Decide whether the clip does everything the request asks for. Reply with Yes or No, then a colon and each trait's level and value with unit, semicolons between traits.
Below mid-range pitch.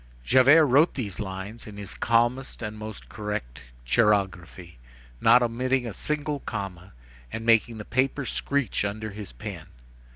Yes: low, 110 Hz